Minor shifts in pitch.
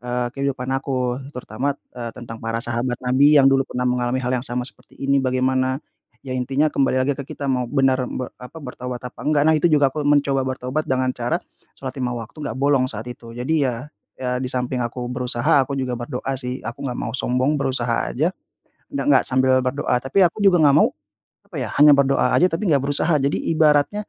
Yes: narrow, 2.2 semitones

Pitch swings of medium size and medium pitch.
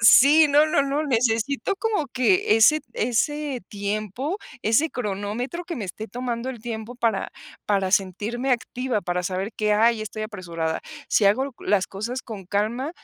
No: average, 4.5 semitones; high, 230 Hz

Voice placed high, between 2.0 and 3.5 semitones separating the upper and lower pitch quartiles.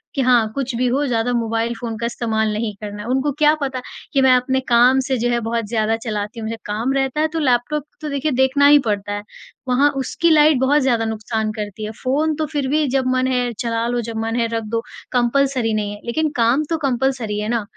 Yes: high, 245 Hz; average, 3.2 semitones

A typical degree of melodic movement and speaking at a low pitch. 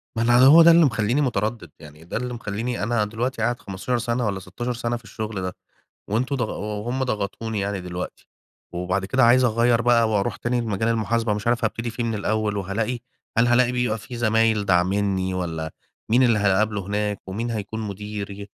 Yes: average, 3.1 semitones; low, 110 Hz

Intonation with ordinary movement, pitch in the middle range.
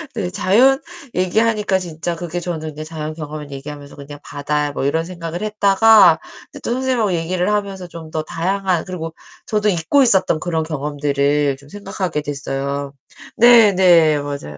Yes: average, 4.7 semitones; medium, 165 Hz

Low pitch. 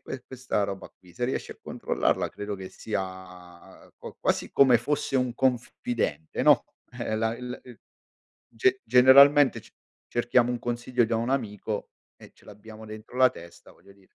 Yes: low, 120 Hz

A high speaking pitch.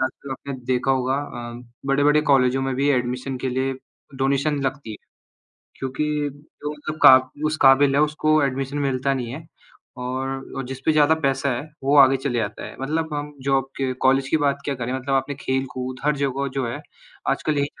No: low, 135 Hz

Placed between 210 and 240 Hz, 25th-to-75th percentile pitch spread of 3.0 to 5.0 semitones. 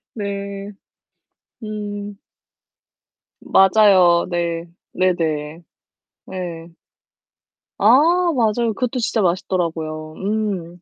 No: high, 190 Hz; average, 3.4 semitones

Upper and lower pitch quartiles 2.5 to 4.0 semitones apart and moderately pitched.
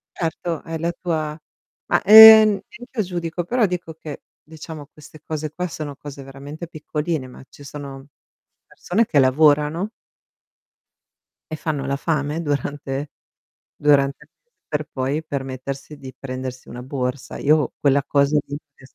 Yes: average, 2.9 semitones; medium, 150 Hz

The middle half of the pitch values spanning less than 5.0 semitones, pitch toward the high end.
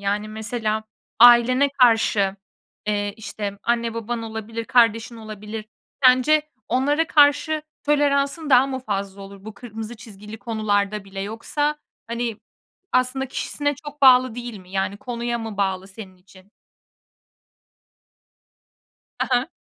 Yes: average, 3.6 semitones; high, 230 Hz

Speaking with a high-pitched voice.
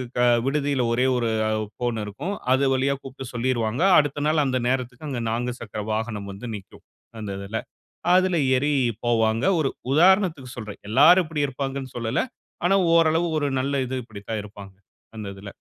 No: low, 130 Hz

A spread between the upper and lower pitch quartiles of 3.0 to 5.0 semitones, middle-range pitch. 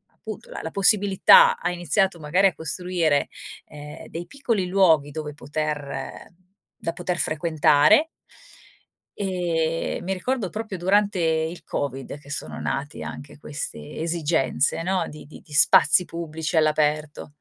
Yes: average, 3.9 semitones; medium, 165 Hz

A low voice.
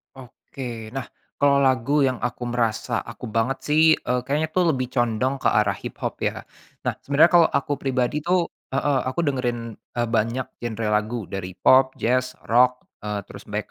Yes: low, 125 Hz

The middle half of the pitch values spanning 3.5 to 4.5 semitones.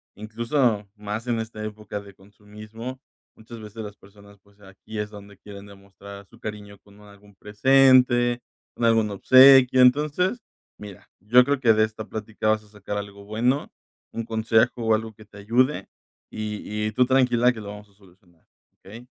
No: average, 2.8 semitones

